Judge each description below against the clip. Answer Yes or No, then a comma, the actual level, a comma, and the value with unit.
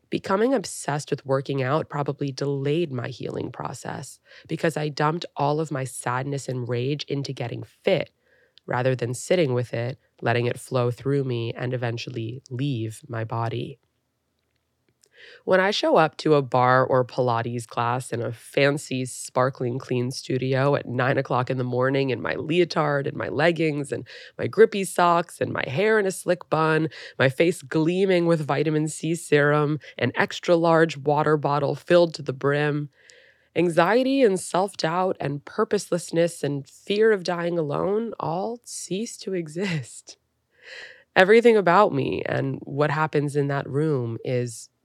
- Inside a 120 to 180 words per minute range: Yes, average, 155 wpm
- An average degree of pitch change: Yes, average, 4.6 semitones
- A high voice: No, medium, 145 Hz